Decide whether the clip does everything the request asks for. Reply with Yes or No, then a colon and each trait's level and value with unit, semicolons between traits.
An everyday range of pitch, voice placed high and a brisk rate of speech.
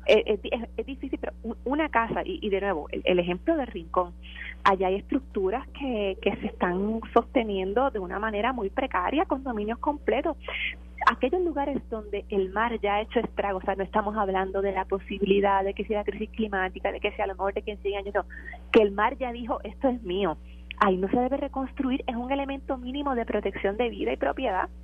Yes: average, 4.5 semitones; high, 215 Hz; fast, 215 wpm